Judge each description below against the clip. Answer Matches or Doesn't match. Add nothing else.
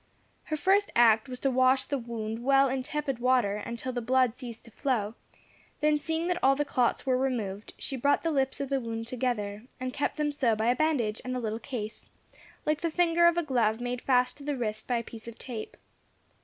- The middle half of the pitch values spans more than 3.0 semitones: Matches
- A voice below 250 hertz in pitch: Doesn't match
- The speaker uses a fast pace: Matches